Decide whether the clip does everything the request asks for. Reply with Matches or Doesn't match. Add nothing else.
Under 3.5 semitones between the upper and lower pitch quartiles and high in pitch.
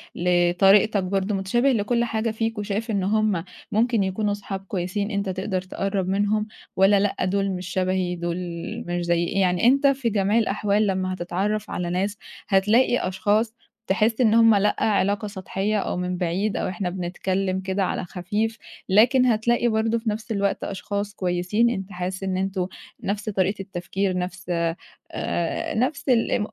Matches